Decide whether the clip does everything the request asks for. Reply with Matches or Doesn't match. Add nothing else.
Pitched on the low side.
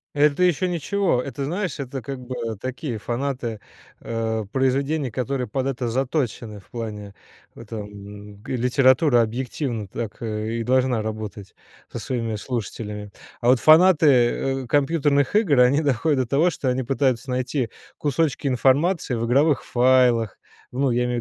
Matches